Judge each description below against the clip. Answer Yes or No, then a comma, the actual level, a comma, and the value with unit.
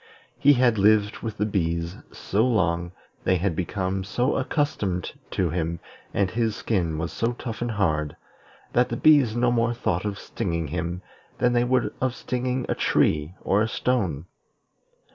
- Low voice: Yes, low, 105 Hz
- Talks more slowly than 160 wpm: No, average, 165 wpm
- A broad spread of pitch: Yes, wide, 5.7 semitones